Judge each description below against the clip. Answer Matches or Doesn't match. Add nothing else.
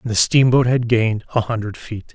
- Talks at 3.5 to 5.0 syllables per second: Doesn't match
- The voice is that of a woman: Doesn't match